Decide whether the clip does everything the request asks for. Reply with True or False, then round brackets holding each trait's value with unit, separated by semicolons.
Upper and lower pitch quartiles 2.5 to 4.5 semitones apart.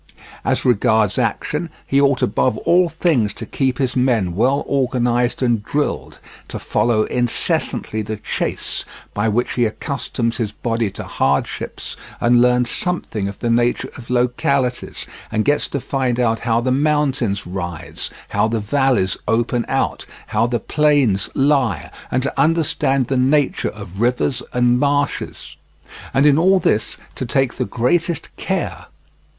True (3.6 semitones)